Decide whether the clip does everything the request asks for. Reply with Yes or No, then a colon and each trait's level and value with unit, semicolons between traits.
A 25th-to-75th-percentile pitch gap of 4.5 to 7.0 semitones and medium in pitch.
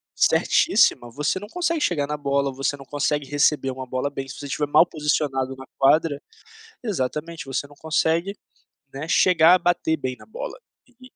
No: average, 3.5 semitones; medium, 150 Hz